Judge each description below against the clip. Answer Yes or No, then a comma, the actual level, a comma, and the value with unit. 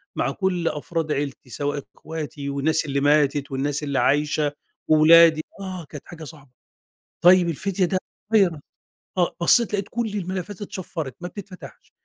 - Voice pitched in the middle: Yes, medium, 160 Hz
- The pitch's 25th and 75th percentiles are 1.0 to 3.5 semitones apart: No, average, 4.0 semitones